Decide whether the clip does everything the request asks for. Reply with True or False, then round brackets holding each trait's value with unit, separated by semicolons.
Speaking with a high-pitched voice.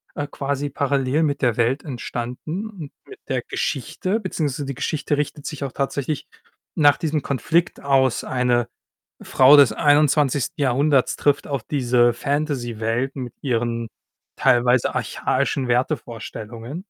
False (140 Hz)